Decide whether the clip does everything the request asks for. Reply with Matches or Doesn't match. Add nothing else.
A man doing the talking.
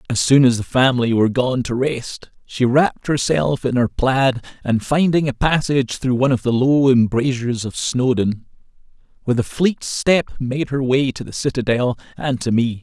Matches